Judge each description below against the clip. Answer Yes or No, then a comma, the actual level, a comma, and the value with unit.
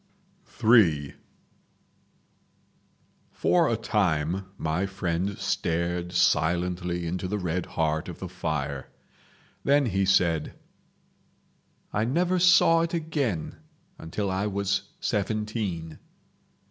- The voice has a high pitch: No, very low, 95 Hz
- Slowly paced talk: Yes, slow, 95 wpm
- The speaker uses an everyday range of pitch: Yes, average, 4.3 semitones